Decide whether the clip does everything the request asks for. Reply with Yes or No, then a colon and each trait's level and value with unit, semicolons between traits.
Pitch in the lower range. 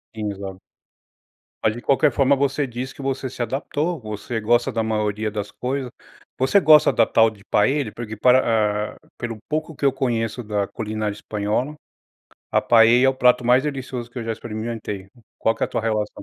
Yes: low, 120 Hz